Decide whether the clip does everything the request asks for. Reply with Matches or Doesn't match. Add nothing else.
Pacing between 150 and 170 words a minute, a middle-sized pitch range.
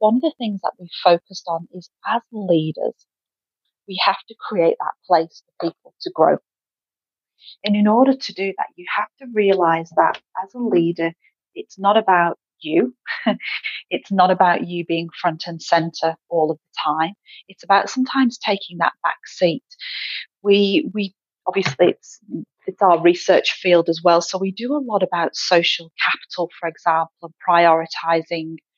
Matches